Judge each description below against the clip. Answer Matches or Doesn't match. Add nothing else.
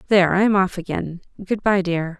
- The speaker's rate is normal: Doesn't match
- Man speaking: Doesn't match